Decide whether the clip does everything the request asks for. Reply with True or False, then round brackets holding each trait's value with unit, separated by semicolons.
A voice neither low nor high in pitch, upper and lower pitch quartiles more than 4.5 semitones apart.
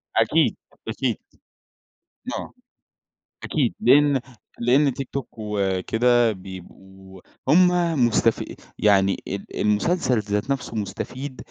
False (115 Hz; 5.2 semitones)